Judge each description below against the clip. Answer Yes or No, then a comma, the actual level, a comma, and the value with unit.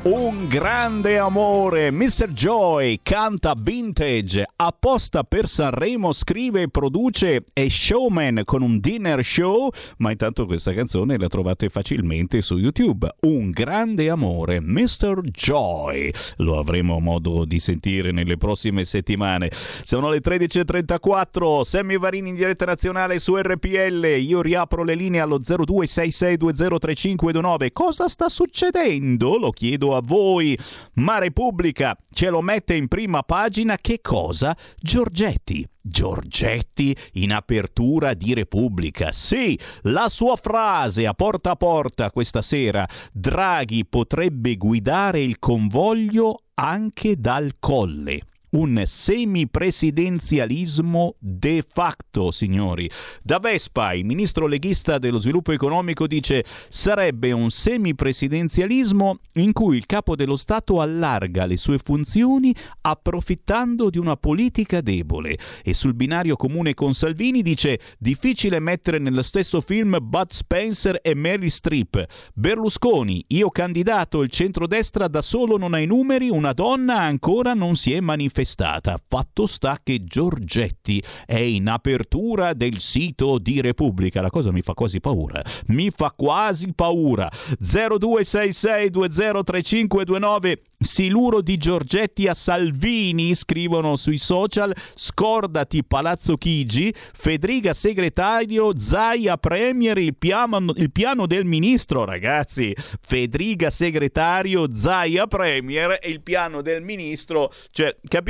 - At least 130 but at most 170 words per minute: No, average, 120 wpm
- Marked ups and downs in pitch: Yes, wide, 7.4 semitones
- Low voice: No, medium, 165 Hz